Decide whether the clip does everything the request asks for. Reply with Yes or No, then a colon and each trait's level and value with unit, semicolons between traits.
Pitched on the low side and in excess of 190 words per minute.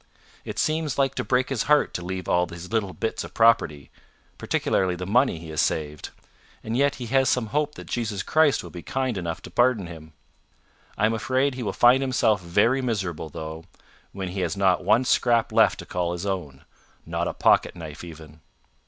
Yes: low, 100 Hz; average, 200 wpm